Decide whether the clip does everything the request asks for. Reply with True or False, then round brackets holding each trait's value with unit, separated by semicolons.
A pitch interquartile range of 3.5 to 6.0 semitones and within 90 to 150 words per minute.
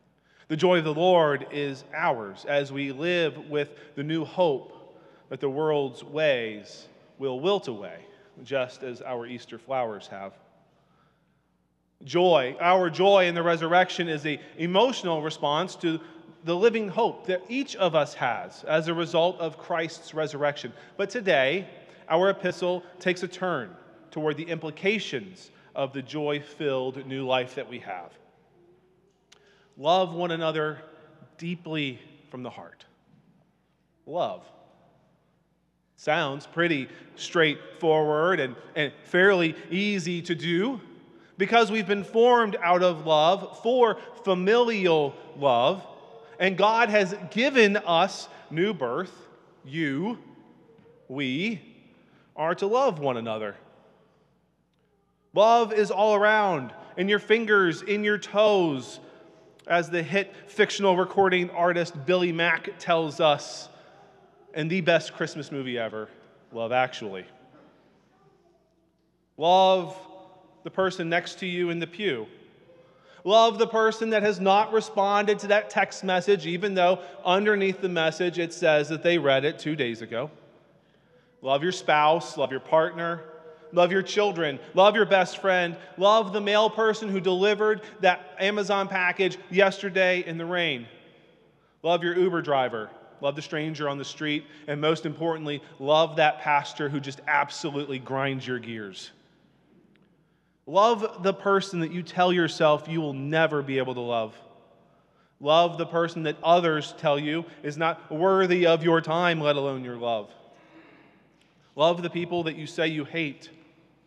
True (3.9 semitones; 135 wpm)